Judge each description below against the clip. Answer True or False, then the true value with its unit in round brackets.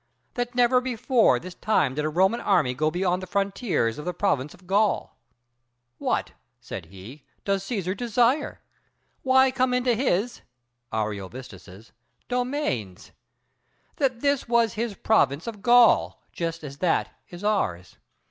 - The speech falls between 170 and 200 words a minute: False (140 wpm)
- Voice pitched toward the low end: False (195 Hz)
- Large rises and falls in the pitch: True (8.6 semitones)